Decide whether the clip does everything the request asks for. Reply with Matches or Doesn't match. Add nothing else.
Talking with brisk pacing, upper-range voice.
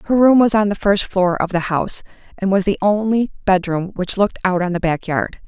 Matches